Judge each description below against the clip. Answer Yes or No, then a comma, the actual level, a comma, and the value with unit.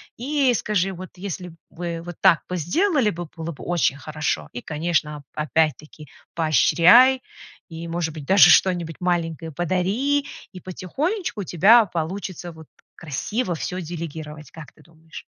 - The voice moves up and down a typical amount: Yes, average, 3.3 semitones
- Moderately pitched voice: Yes, medium, 170 Hz